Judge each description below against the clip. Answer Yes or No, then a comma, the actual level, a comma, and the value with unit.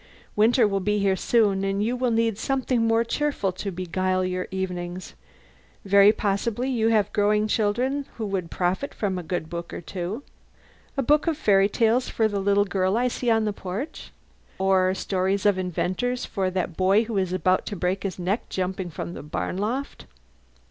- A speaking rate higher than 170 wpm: Yes, average, 185 wpm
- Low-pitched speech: No, high, 200 Hz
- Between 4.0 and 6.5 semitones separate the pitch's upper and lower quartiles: No, average, 3.4 semitones